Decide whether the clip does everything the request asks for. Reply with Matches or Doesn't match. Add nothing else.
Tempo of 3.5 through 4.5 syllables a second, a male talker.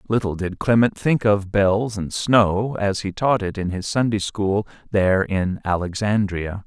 Matches